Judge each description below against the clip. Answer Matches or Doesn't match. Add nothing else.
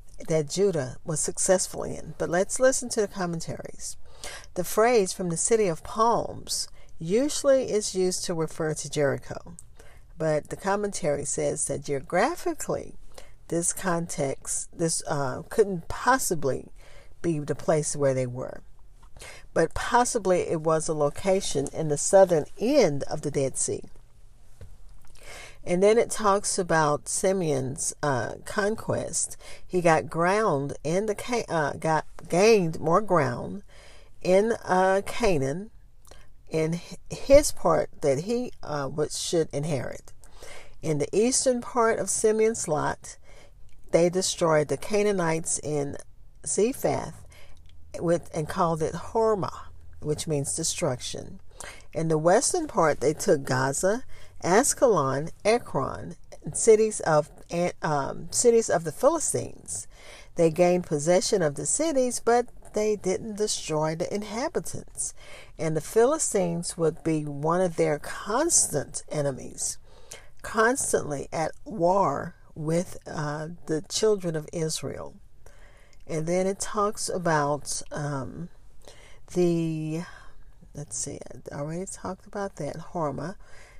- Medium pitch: Matches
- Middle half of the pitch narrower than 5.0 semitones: Doesn't match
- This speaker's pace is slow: Matches